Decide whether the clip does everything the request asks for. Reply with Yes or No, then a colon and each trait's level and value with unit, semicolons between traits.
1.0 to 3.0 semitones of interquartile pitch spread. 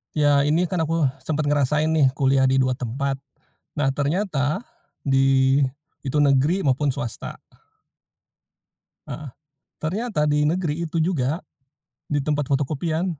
Yes: average, 2.7 semitones